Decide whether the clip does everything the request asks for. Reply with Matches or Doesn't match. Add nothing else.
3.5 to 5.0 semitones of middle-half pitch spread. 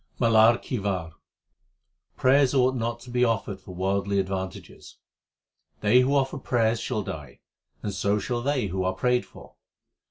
Matches